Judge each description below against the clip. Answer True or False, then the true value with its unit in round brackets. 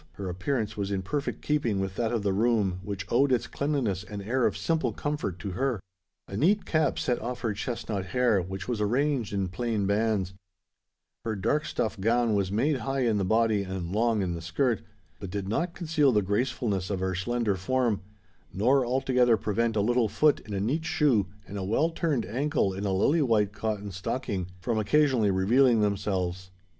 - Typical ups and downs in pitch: True (4.6 semitones)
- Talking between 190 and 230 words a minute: True (195 wpm)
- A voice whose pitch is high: False (110 Hz)